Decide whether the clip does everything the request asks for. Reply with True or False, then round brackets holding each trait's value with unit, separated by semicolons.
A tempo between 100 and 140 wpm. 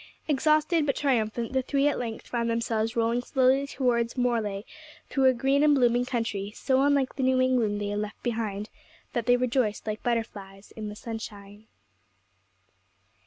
False (165 wpm)